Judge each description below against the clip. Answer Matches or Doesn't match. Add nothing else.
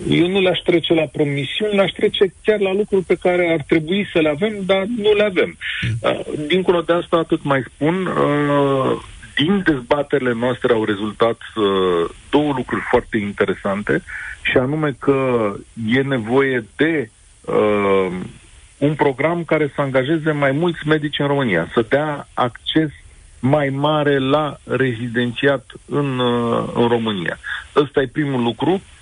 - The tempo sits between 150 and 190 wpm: Doesn't match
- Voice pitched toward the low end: Doesn't match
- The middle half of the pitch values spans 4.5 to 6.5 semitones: Matches